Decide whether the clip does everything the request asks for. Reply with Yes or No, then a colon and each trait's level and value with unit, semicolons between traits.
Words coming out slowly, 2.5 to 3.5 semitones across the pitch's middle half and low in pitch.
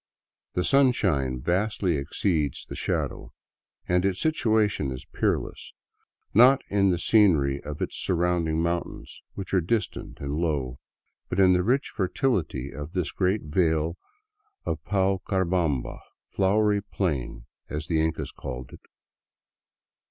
No: slow, 130 wpm; average, 4.7 semitones; very low, 90 Hz